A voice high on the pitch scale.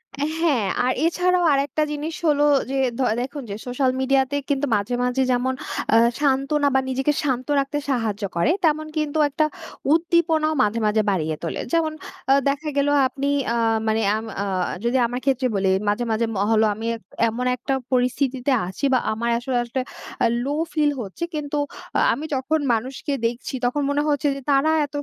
Yes: very high, 270 Hz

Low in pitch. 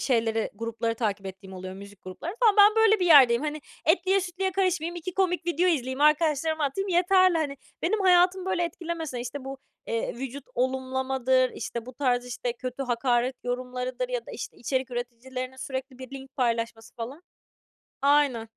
No: very high, 265 Hz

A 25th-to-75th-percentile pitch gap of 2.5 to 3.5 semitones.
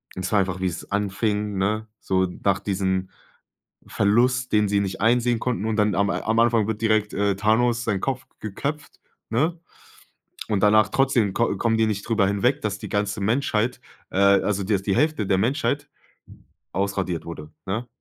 Yes: average, 2.9 semitones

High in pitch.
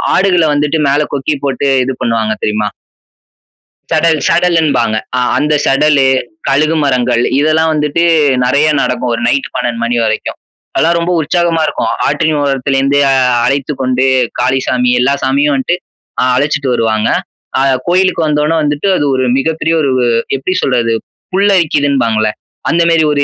No: medium, 145 Hz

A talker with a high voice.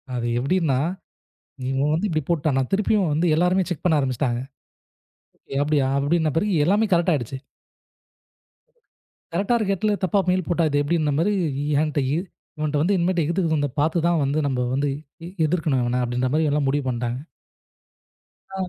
No: medium, 155 Hz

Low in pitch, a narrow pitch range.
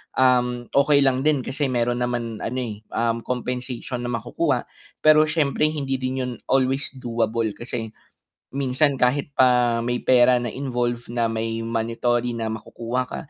Yes: low, 125 Hz; narrow, 2.0 semitones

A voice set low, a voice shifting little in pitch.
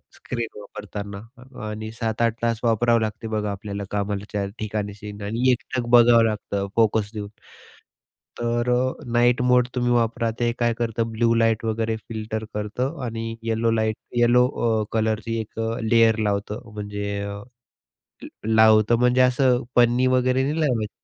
Yes: low, 115 Hz; narrow, 2.1 semitones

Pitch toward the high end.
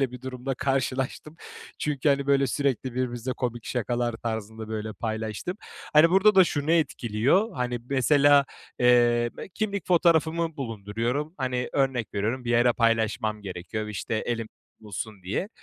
No: low, 125 Hz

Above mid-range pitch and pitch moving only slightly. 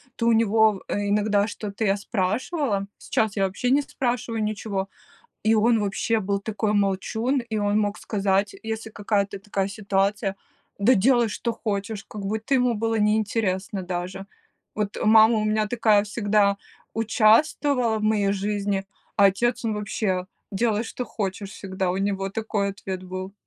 Yes: high, 210 Hz; narrow, 2.1 semitones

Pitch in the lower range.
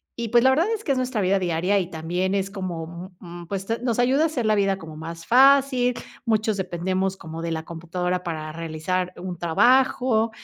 No: high, 190 Hz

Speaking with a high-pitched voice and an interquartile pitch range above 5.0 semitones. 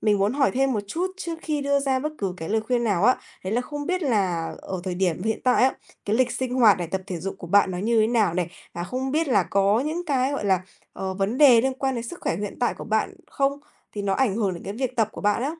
Yes: high, 225 Hz; wide, 5.4 semitones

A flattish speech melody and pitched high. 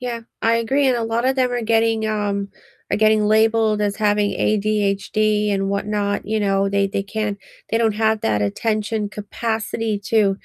Yes: narrow, 1.8 semitones; high, 215 Hz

